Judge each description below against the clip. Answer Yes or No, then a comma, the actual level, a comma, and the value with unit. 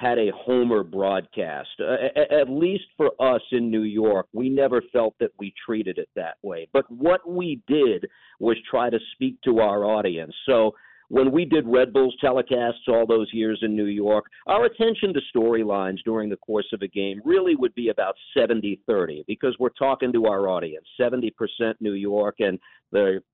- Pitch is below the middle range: Yes, low, 115 Hz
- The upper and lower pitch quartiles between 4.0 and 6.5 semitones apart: Yes, average, 4.4 semitones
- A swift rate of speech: No, average, 190 wpm